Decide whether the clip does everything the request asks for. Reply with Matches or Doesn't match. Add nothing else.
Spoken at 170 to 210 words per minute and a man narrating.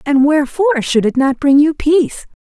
Doesn't match